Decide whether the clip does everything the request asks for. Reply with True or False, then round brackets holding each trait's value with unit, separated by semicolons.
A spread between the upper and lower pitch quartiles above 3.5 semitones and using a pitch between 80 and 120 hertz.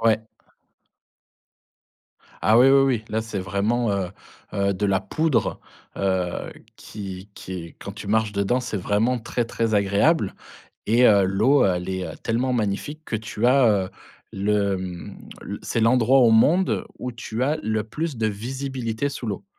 True (3.9 semitones; 110 Hz)